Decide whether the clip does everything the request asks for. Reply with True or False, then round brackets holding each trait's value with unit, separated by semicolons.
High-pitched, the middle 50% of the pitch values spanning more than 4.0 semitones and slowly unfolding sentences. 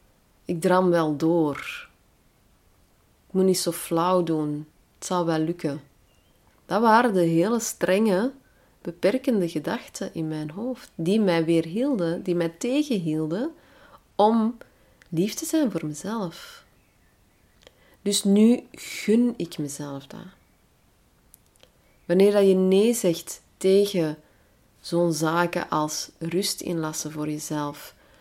False (170 Hz; 4.9 semitones; 115 wpm)